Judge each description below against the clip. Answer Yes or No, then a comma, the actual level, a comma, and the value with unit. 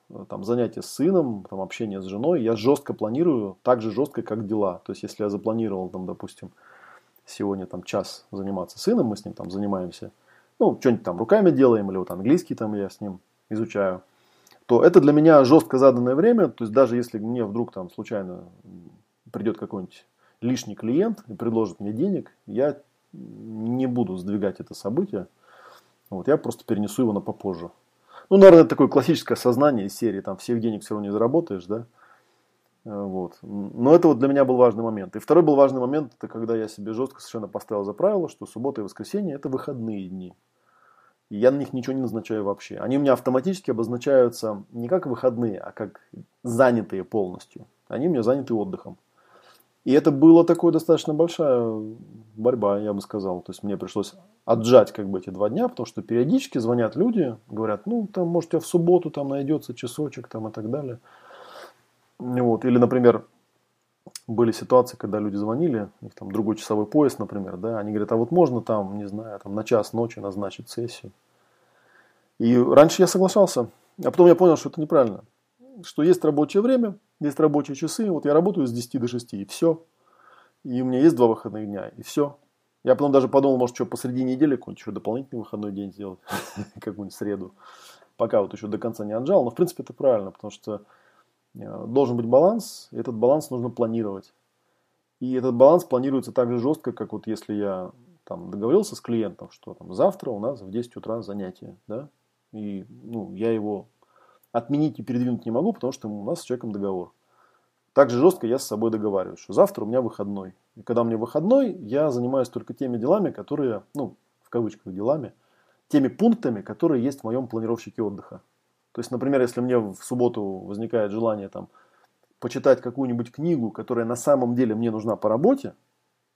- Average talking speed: No, fast, 185 wpm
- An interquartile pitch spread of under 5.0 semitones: Yes, average, 4.5 semitones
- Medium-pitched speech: No, low, 120 Hz